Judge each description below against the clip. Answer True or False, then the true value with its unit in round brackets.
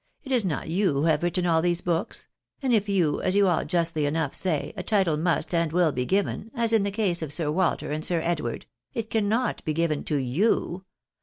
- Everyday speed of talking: False (220 wpm)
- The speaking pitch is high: False (175 Hz)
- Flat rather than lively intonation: False (4.3 semitones)